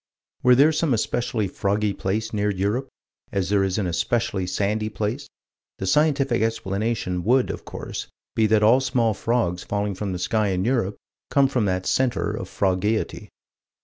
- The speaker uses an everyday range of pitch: Yes, average, 3.8 semitones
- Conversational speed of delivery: Yes, average, 165 wpm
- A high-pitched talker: No, low, 105 Hz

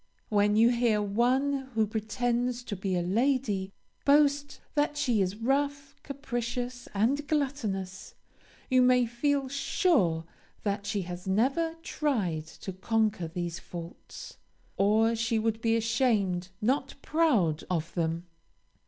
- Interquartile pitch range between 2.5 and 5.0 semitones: No, wide, 5.6 semitones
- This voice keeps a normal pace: No, slow, 125 wpm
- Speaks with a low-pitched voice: No, high, 230 Hz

